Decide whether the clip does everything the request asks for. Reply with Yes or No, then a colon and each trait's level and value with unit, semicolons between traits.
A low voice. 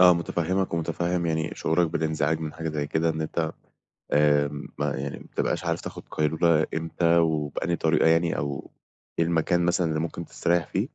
Yes: very low, 80 Hz